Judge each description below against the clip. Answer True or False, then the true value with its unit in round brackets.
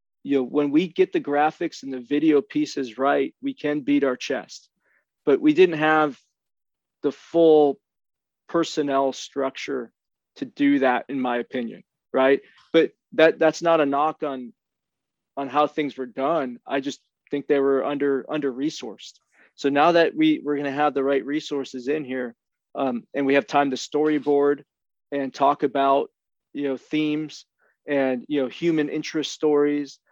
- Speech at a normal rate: True (165 wpm)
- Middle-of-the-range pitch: True (145 Hz)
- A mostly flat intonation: True (2.1 semitones)